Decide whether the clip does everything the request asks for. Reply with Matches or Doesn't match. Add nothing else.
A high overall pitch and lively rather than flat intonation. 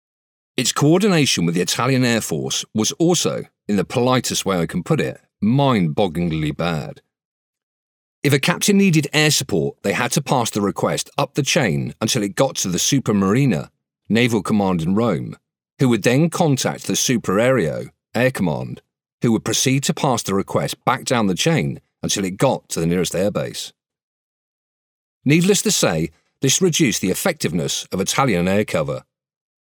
Doesn't match